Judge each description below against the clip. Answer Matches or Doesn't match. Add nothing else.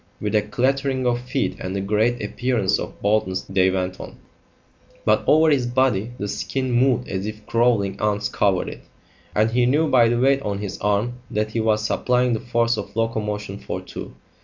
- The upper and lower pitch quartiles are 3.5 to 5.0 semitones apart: Doesn't match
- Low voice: Matches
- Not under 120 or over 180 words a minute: Doesn't match